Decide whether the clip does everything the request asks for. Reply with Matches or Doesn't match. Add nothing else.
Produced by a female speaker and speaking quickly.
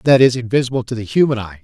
Doesn't match